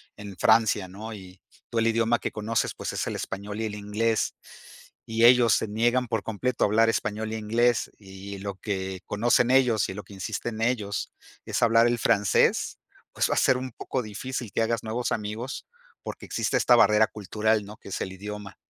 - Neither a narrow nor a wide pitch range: No, narrow, 2.1 semitones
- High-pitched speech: No, low, 110 Hz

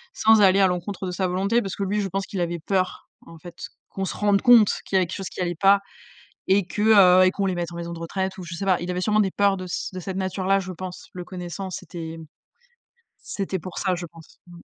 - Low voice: No, medium, 185 Hz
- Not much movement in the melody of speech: Yes, narrow, 1.8 semitones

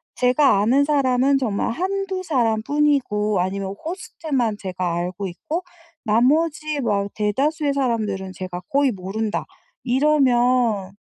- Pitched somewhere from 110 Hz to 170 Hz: No, high, 245 Hz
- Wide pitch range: Yes, wide, 6.1 semitones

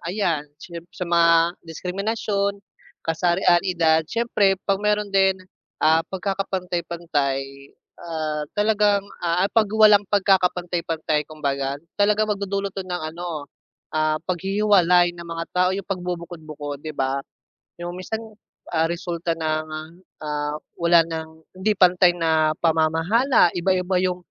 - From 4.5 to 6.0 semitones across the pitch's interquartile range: No, average, 3.4 semitones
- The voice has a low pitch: No, medium, 175 Hz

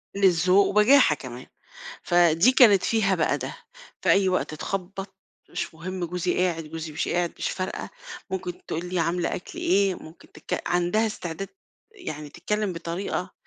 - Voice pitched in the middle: Yes, medium, 180 Hz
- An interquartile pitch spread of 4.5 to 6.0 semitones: No, average, 2.8 semitones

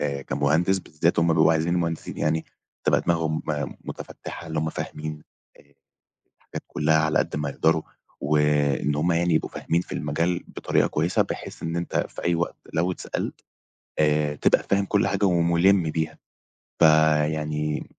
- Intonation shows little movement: Yes, narrow, 2.0 semitones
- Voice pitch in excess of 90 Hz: No, very low, 80 Hz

